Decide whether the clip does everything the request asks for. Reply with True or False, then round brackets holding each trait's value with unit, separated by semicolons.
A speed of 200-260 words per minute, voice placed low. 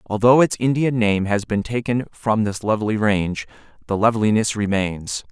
False (160 wpm; 110 Hz)